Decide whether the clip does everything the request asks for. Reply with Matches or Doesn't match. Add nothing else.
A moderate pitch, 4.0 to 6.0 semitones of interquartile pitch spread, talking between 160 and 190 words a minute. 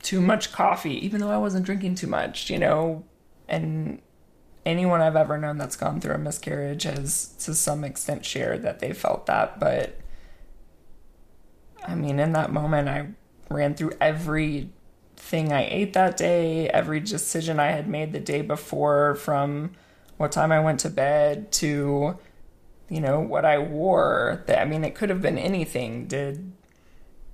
Doesn't match